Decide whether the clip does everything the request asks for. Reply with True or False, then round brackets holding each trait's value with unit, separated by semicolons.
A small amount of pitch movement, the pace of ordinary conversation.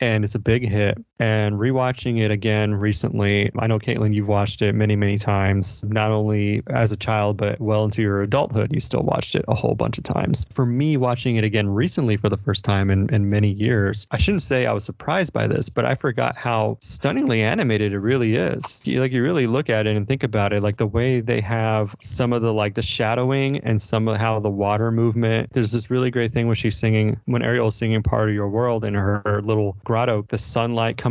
False (2.2 semitones; 235 wpm)